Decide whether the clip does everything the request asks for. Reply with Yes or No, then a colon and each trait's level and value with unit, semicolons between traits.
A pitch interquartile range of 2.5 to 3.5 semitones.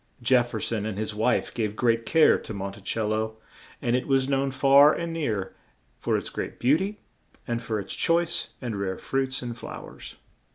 No: average, 3.9 semitones